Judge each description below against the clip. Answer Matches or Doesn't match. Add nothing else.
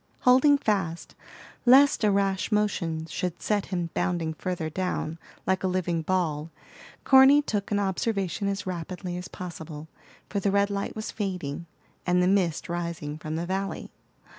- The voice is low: Doesn't match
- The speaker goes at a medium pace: Matches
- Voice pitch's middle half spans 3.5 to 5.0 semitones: Doesn't match